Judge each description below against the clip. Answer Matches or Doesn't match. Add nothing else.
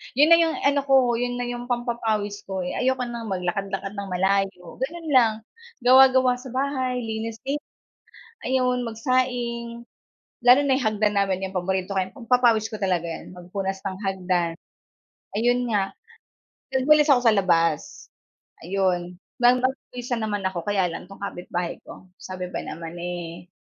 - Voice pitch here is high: Matches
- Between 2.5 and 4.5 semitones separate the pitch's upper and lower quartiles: Doesn't match